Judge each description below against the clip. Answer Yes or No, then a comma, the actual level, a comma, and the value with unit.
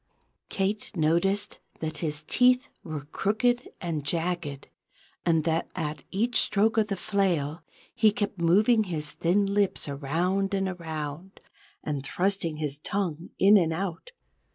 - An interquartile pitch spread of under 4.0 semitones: No, average, 4.4 semitones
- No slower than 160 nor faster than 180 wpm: No, slow, 135 wpm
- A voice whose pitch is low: No, medium, 175 Hz